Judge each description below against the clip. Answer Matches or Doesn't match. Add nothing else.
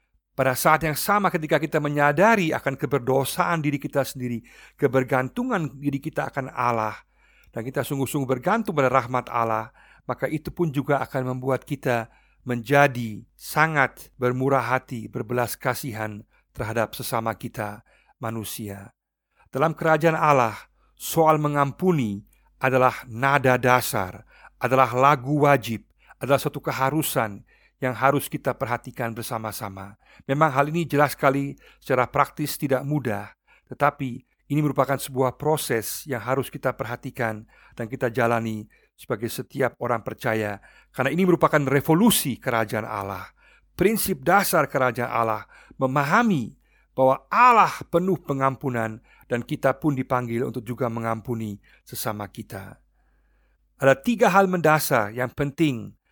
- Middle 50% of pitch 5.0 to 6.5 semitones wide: Doesn't match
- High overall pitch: Doesn't match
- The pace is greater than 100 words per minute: Matches